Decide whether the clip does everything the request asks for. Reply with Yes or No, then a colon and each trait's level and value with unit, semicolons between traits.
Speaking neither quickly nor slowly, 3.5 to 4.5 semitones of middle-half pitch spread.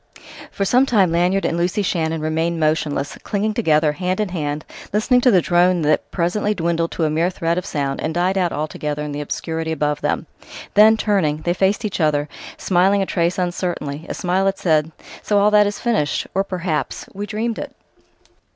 Yes: average, 195 wpm; average, 4.0 semitones